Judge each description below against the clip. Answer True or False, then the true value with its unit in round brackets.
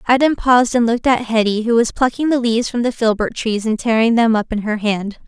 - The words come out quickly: True (250 wpm)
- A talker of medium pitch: False (230 Hz)